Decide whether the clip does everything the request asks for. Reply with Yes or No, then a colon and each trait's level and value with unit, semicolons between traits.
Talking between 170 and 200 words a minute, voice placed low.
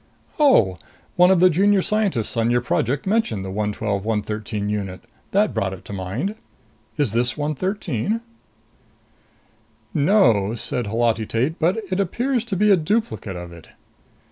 No: average, 145 wpm; low, 125 Hz